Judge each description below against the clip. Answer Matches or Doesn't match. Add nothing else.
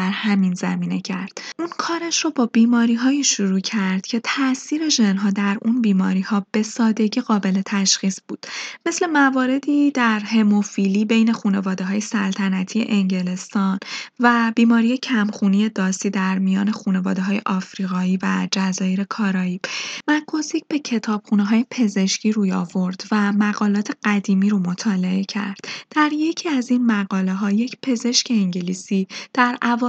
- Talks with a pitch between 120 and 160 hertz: Doesn't match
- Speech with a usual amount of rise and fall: Matches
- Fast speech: Doesn't match